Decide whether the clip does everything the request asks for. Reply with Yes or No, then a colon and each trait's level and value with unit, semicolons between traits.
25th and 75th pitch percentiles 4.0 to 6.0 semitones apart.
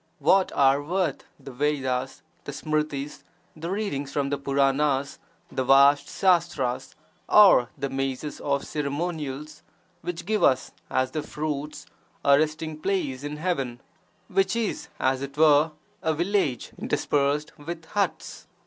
No: average, 3.0 semitones